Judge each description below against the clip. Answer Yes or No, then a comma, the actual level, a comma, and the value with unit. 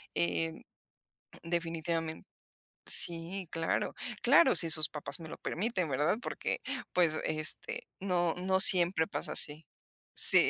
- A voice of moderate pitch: Yes, medium, 165 Hz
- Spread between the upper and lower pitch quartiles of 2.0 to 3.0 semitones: Yes, narrow, 2.4 semitones